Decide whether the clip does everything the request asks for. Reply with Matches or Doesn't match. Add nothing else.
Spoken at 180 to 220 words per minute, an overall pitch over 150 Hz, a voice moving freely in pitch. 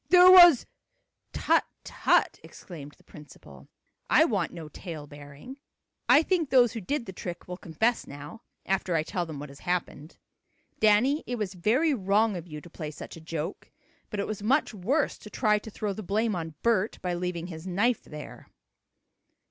Matches